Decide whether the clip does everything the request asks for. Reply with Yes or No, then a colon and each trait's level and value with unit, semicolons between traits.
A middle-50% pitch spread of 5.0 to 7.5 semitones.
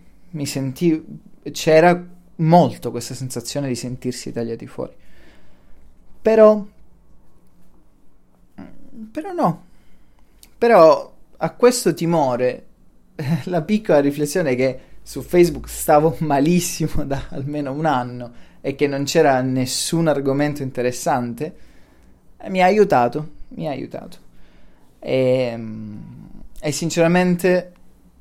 Yes: wide, 5.5 semitones